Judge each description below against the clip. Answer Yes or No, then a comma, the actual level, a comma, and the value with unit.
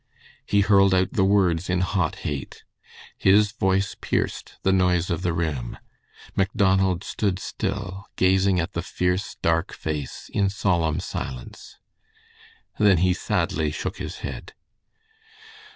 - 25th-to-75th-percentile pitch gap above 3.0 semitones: No, narrow, 2.5 semitones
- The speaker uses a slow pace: Yes, slow, 130 wpm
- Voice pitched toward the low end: Yes, very low, 95 Hz